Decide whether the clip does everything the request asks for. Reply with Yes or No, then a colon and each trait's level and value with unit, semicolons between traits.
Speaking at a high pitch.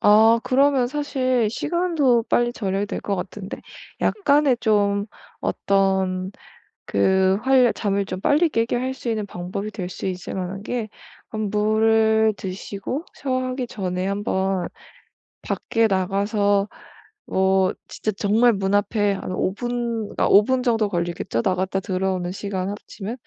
Yes: high, 205 Hz